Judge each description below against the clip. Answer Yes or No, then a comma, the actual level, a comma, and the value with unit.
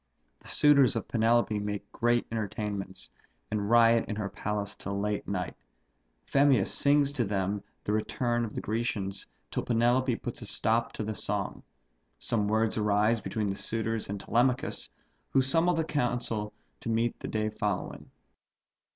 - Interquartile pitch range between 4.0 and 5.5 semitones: No, narrow, 2.5 semitones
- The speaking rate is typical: Yes, average, 150 wpm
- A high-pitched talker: No, low, 110 Hz